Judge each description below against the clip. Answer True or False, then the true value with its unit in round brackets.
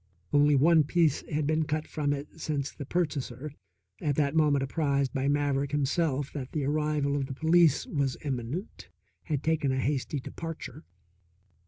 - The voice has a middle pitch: True (145 Hz)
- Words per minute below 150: False (160 wpm)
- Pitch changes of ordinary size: False (2.0 semitones)